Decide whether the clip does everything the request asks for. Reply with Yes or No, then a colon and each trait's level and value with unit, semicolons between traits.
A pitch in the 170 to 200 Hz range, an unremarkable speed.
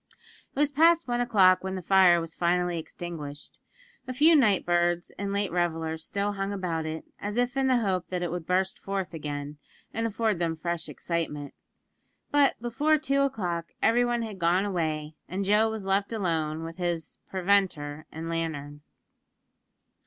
Yes: medium, 185 Hz; average, 165 wpm